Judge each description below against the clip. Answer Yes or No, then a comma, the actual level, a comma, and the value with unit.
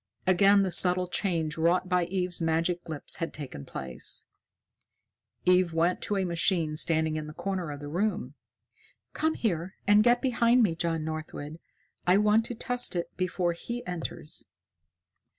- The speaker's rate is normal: Yes, average, 155 wpm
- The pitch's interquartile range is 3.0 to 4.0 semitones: Yes, average, 3.4 semitones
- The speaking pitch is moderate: Yes, medium, 180 Hz